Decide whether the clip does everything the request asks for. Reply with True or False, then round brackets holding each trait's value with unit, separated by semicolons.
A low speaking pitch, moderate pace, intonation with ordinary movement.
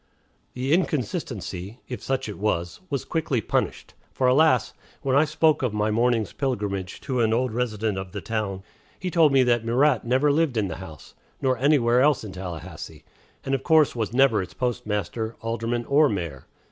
True (120 Hz; 180 wpm; 4.4 semitones)